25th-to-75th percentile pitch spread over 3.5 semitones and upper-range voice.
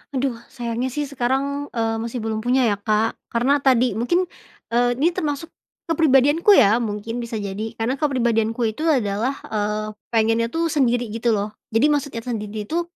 Yes: average, 3.9 semitones; high, 240 Hz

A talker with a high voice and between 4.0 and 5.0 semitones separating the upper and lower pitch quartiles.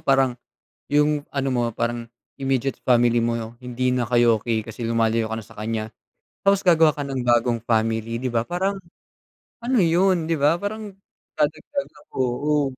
No: low, 125 Hz; average, 4.4 semitones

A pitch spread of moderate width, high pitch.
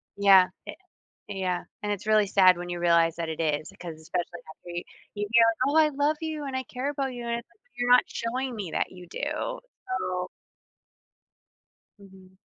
No: wide, 6.7 semitones; high, 200 Hz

